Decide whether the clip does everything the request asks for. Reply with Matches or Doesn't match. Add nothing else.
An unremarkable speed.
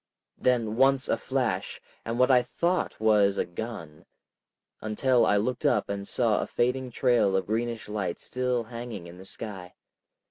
Matches